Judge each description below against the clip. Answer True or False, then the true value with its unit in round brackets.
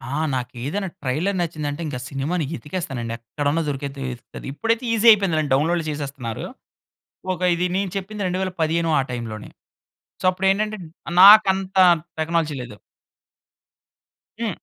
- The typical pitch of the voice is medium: True (165 Hz)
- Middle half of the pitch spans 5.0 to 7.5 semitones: True (5.3 semitones)